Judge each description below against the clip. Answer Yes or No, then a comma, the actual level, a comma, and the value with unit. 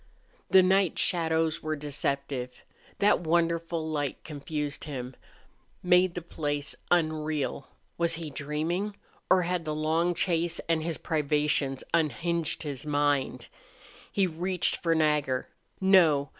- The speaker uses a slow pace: Yes, slow, 120 wpm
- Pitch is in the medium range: Yes, medium, 160 Hz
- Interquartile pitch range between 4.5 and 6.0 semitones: No, average, 2.7 semitones